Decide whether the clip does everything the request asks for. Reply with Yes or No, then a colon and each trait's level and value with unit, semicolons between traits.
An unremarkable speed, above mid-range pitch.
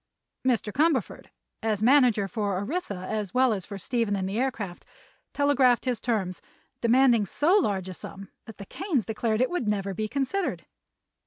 Yes: average, 165 wpm; high, 225 Hz